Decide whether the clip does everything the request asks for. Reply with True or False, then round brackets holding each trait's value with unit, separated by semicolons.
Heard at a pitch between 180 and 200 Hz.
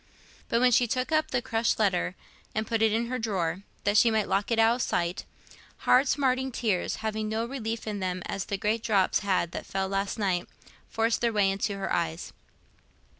False (215 Hz)